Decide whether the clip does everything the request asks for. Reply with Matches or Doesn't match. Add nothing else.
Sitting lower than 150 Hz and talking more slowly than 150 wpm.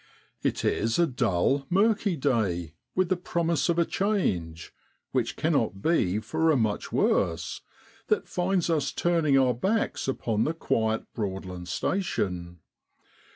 Matches